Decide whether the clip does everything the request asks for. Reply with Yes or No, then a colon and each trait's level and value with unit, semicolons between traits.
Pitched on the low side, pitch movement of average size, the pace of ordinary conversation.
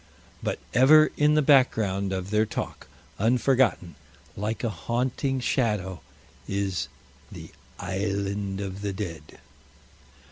No: low, 105 Hz; average, 4.6 semitones; slow, 110 wpm